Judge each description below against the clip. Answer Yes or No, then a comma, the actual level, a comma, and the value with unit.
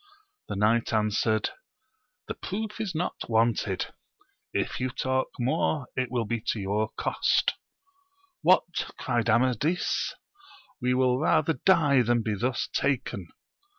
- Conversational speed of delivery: No, slow, 125 wpm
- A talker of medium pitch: No, low, 125 Hz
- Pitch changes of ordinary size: Yes, average, 3.9 semitones